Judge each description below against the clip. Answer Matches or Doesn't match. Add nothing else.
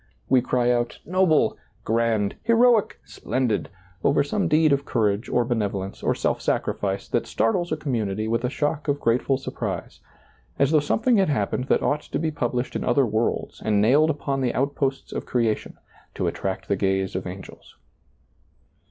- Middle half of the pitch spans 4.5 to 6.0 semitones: Matches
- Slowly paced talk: Doesn't match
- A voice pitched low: Matches